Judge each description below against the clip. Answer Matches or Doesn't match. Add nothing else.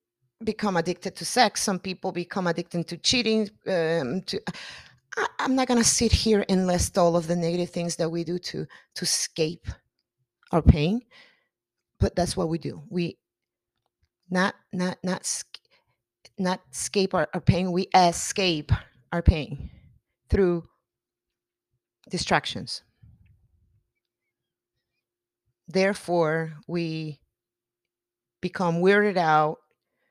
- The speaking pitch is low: Doesn't match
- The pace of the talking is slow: Matches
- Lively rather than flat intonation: Matches